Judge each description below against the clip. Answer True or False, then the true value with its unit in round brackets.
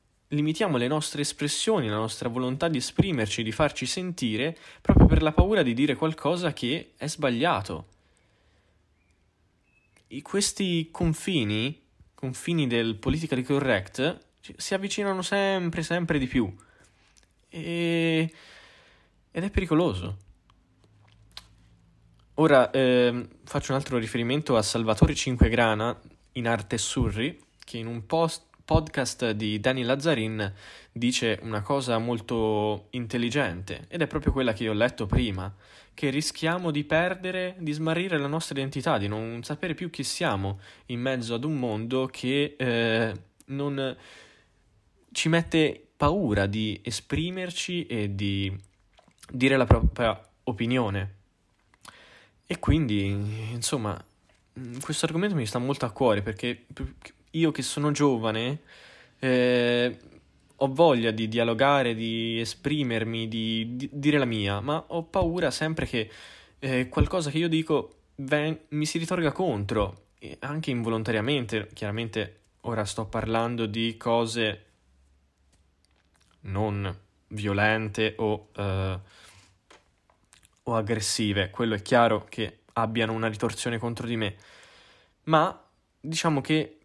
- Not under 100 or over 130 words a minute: True (120 wpm)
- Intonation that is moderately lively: False (5.7 semitones)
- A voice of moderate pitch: False (120 Hz)